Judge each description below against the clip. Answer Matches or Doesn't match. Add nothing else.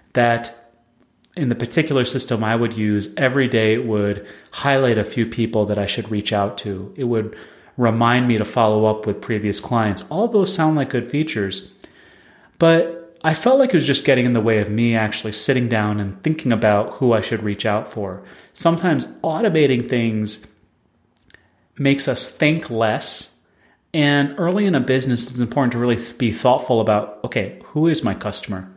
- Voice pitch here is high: Doesn't match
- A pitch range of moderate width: Matches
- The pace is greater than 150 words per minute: Matches